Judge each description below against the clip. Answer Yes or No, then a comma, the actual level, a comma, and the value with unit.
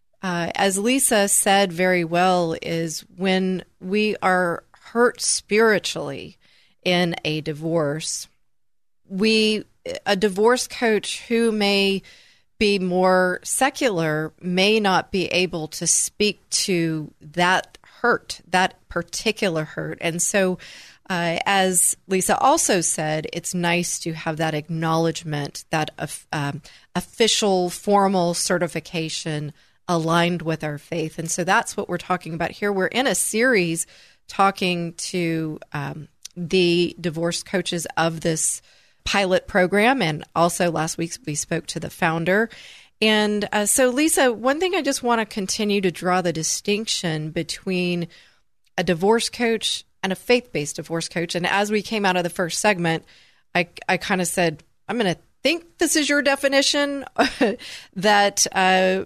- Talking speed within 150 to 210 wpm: No, average, 140 wpm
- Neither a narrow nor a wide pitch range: Yes, average, 3.8 semitones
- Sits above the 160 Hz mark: Yes, medium, 185 Hz